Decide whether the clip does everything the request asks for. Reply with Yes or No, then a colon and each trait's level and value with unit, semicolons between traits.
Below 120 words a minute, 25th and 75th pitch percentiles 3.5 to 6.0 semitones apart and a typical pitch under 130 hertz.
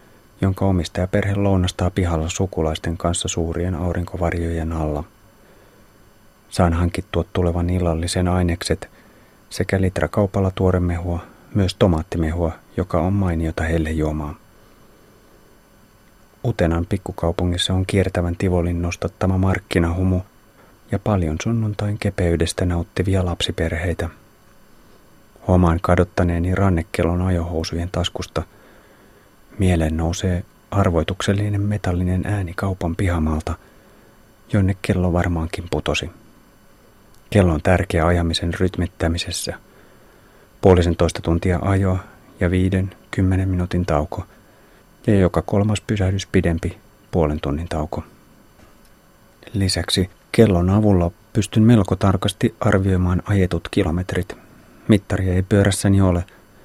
No: slow, 95 wpm; average, 2.8 semitones; very low, 90 Hz